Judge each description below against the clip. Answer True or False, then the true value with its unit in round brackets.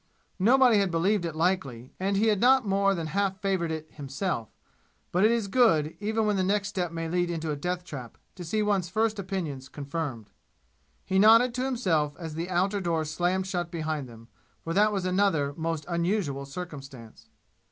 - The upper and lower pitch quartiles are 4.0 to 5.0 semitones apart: True (4.3 semitones)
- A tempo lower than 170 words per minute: False (185 wpm)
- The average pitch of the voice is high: False (180 Hz)